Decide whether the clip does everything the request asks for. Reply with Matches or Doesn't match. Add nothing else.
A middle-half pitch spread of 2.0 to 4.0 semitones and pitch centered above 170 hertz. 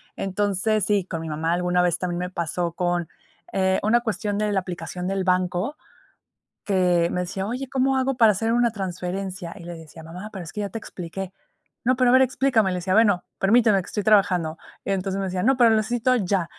Matches